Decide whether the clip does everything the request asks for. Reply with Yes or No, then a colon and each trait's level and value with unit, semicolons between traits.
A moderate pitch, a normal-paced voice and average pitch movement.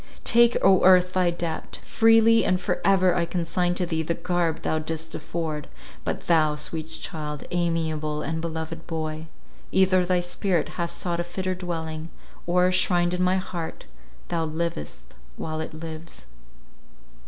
No: medium, 170 Hz; average, 155 wpm; narrow, 2.3 semitones